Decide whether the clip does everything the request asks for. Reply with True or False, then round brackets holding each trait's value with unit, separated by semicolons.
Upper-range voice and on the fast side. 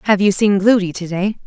True (195 Hz; 245 wpm)